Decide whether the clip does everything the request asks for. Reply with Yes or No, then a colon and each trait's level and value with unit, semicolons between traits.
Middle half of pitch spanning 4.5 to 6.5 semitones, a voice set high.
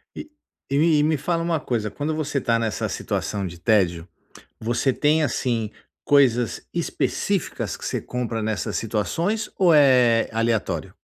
No: average, 5.3 semitones; low, 125 Hz